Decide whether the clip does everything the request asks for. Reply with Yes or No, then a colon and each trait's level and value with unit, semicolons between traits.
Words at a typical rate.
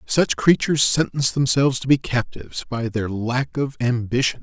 Yes: average, 165 wpm